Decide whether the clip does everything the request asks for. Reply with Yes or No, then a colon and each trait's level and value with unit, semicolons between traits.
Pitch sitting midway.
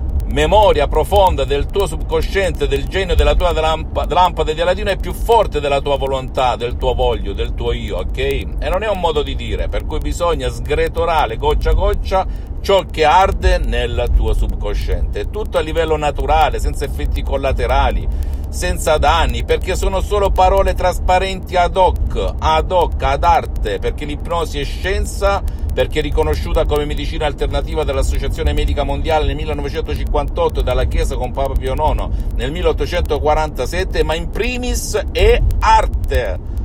Yes: medium, 160 Hz